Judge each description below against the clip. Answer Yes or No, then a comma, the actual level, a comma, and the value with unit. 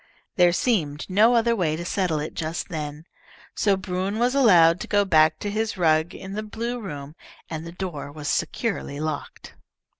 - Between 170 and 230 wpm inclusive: Yes, average, 180 wpm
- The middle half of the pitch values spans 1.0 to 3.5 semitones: No, average, 5.0 semitones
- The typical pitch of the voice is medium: Yes, medium, 180 Hz